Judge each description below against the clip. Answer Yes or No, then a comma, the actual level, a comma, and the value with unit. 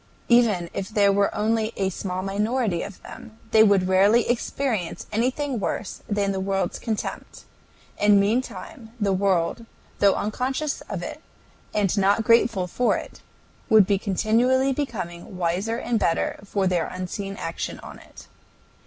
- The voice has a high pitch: Yes, high, 205 Hz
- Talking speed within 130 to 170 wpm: Yes, average, 145 wpm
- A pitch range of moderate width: Yes, average, 3.2 semitones